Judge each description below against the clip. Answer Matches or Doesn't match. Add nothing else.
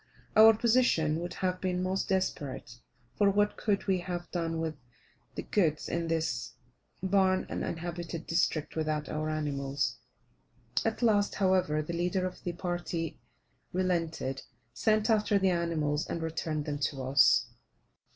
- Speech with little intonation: Doesn't match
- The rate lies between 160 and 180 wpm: Doesn't match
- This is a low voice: Doesn't match